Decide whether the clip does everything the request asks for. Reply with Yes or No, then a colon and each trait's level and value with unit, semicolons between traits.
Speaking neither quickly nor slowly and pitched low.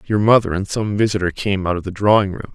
No: fast, 235 wpm; low, 100 Hz